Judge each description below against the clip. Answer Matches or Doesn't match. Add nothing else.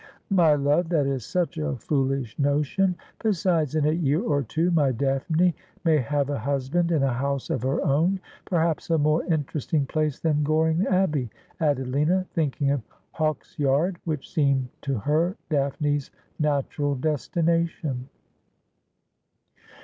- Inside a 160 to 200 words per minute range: Doesn't match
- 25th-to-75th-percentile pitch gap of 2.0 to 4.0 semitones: Matches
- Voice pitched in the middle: Matches